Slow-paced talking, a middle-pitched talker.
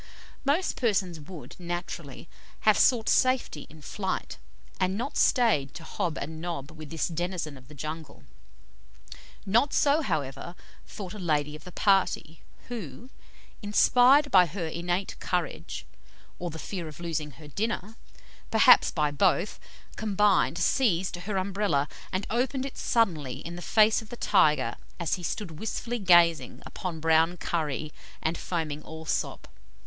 No: average, 145 wpm; medium, 175 Hz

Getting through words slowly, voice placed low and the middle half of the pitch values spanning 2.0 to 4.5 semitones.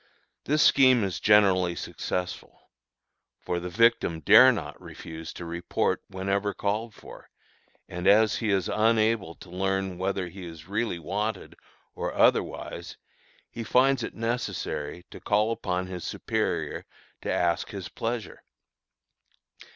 Yes: slow, 130 wpm; low, 100 Hz; average, 3.9 semitones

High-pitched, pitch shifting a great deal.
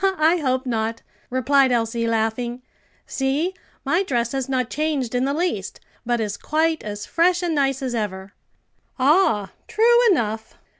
Yes: very high, 260 Hz; wide, 5.7 semitones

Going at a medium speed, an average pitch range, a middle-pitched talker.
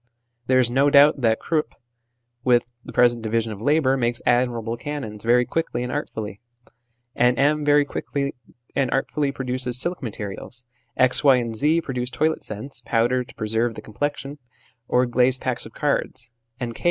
No: average, 170 wpm; average, 3.0 semitones; low, 125 Hz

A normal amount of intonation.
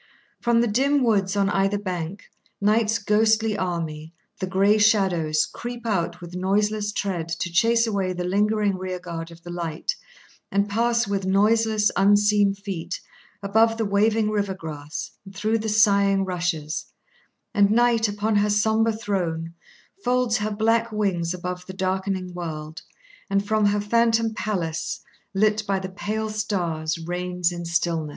Yes: average, 3.3 semitones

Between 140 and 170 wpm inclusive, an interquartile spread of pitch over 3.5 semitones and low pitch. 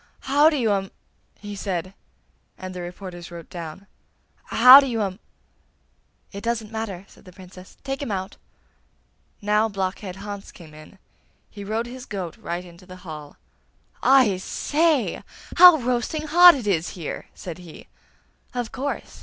No: average, 155 wpm; average, 5.2 semitones; high, 200 Hz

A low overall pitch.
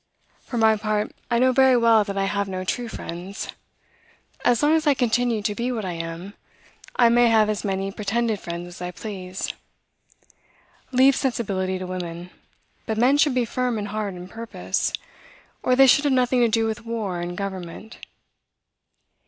No: high, 220 Hz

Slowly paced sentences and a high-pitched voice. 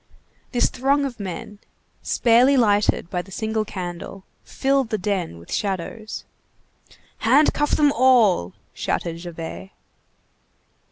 Yes: slow, 110 wpm; high, 210 Hz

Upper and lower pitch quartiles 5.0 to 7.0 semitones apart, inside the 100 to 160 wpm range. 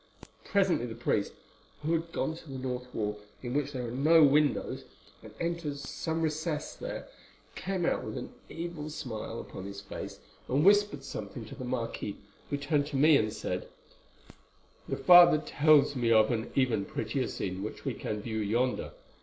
No: wide, 5.5 semitones; average, 175 wpm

